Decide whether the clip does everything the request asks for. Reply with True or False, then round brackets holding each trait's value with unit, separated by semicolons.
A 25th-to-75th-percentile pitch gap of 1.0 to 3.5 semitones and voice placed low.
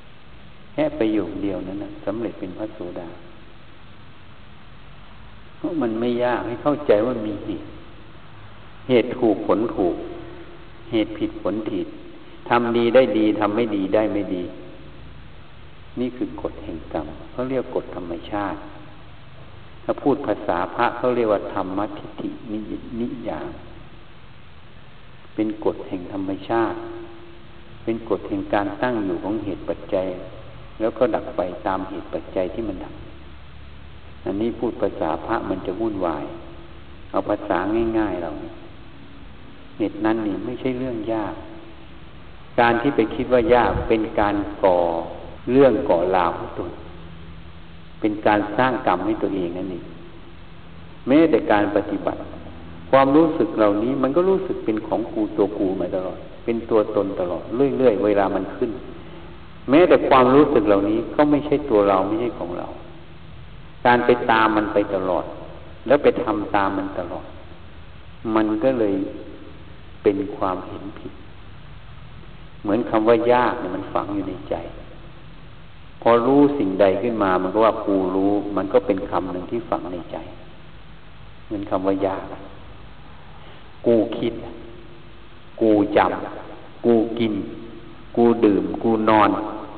False (4.5 semitones; 110 Hz)